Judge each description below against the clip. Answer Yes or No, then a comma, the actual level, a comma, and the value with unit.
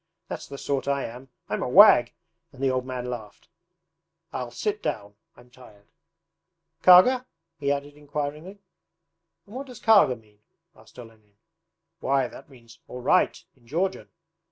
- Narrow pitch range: No, average, 3.9 semitones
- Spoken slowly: No, average, 150 wpm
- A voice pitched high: No, low, 135 Hz